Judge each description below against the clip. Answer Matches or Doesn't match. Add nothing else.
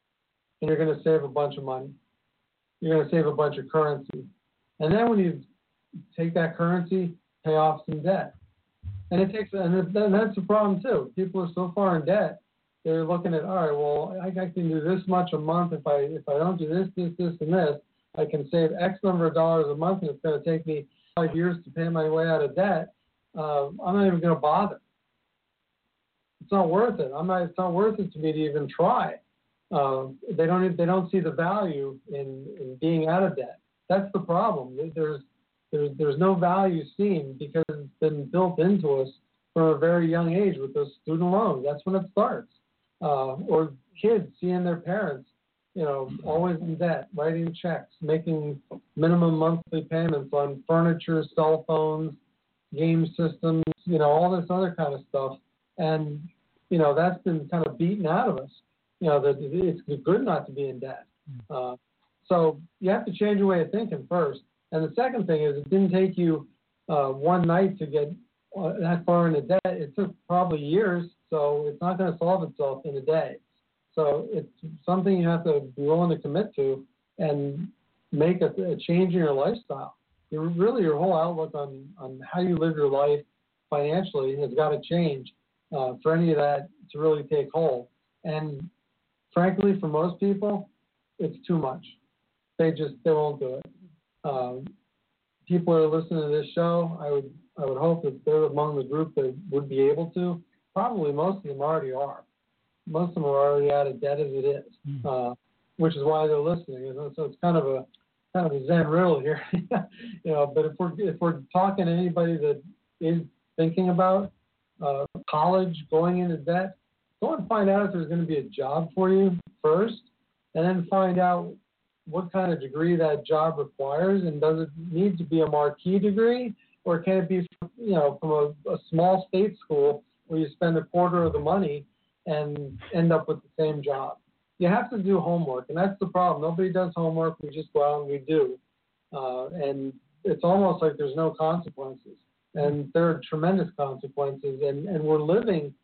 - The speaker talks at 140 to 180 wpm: Doesn't match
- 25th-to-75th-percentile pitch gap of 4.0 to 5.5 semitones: Doesn't match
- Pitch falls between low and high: Matches